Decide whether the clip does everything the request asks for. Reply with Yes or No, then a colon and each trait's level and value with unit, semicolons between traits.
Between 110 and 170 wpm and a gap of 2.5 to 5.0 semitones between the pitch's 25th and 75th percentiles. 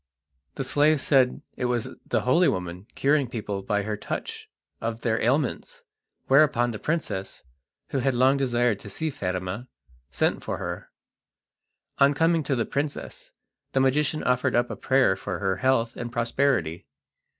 Yes: average, 155 wpm; average, 4.4 semitones